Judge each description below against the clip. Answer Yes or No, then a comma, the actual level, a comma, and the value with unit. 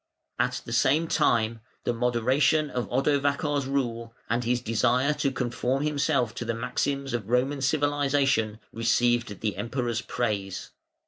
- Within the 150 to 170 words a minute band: No, slow, 135 wpm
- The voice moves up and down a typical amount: Yes, average, 3.3 semitones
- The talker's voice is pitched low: Yes, low, 125 Hz